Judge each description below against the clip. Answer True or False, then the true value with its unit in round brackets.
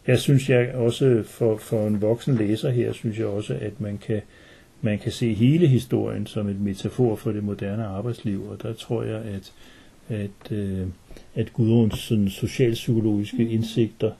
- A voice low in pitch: True (110 Hz)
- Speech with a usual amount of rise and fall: False (2.3 semitones)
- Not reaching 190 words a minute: True (165 wpm)